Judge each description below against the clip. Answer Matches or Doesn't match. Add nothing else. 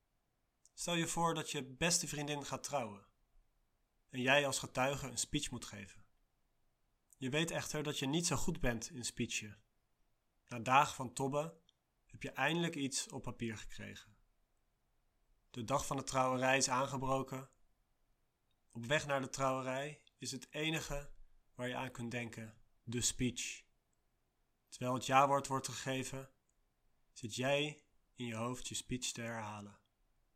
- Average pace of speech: Matches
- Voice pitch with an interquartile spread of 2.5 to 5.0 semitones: Matches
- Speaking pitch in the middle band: Doesn't match